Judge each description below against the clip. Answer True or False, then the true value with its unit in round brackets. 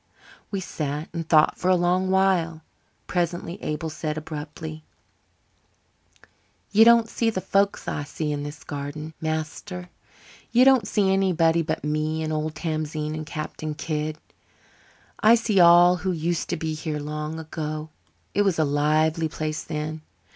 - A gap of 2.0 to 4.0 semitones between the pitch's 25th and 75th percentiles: True (2.8 semitones)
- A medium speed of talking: True (150 wpm)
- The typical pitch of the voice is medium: True (160 Hz)